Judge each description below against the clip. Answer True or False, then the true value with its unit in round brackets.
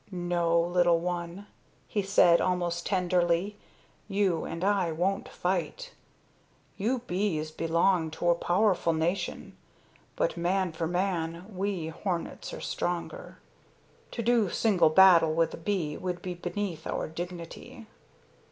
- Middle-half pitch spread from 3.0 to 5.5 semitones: False (2.5 semitones)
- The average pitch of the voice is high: False (175 Hz)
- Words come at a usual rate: False (125 wpm)